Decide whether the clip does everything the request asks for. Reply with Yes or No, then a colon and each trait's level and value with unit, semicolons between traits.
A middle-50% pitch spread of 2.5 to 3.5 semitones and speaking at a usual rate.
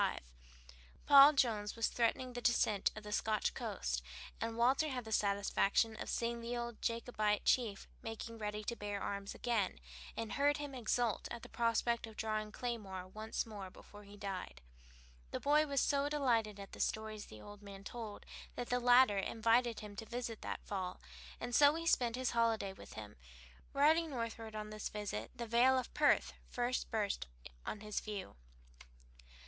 Yes: average, 2.9 semitones; average, 175 wpm